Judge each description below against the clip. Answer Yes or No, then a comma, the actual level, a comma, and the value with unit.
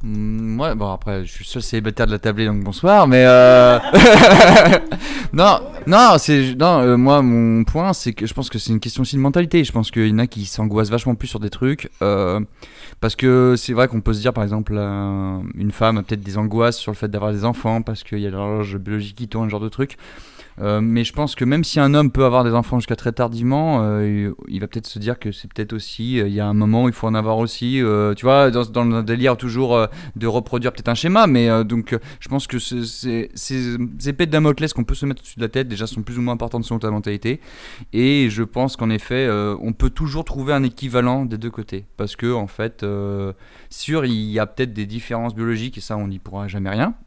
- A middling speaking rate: No, fast, 250 wpm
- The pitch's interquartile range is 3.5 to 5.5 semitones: No, average, 3.0 semitones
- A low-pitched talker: Yes, low, 115 Hz